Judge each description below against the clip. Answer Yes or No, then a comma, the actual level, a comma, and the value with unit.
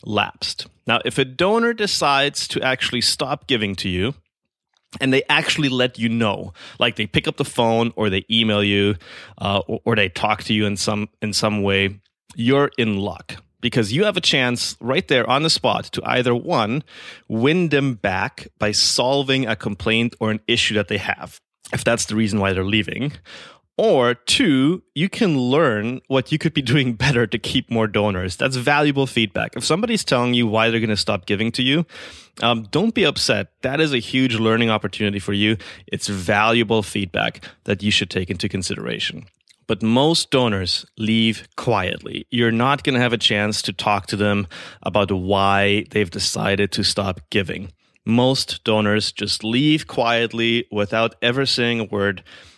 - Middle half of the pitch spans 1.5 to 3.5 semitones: No, average, 4.2 semitones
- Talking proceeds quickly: No, average, 185 wpm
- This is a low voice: Yes, low, 115 Hz